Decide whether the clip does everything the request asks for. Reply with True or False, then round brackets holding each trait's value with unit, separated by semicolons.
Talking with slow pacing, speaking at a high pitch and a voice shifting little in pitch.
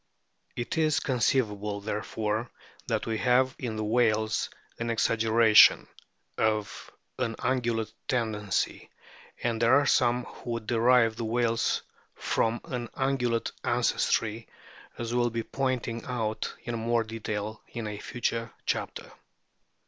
False (125 wpm; 115 Hz; 1.8 semitones)